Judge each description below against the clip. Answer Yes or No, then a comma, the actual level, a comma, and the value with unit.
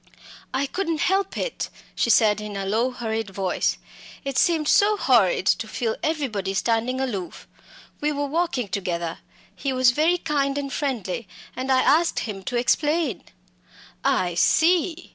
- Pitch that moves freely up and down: Yes, wide, 6.2 semitones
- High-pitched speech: Yes, very high, 255 Hz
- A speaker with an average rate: Yes, average, 150 wpm